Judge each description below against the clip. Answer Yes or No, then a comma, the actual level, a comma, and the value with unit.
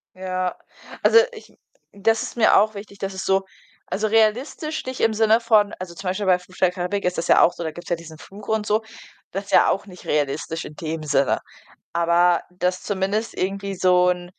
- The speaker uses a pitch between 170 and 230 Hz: Yes, high, 190 Hz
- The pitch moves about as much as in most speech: Yes, average, 3.1 semitones